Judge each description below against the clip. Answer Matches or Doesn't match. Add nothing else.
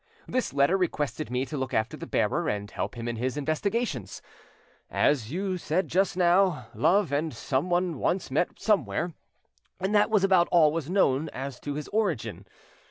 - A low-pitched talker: Doesn't match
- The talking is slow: Doesn't match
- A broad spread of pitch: Matches